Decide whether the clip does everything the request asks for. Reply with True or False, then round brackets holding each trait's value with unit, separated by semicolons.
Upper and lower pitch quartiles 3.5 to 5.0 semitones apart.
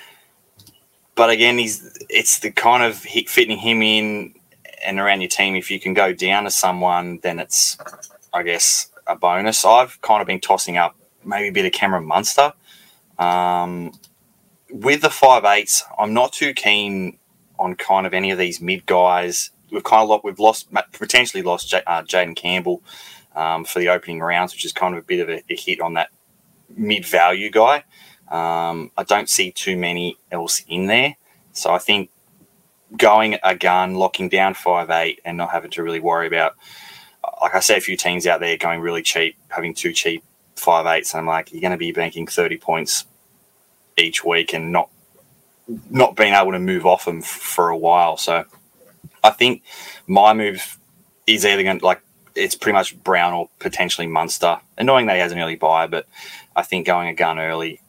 True (4.0 semitones)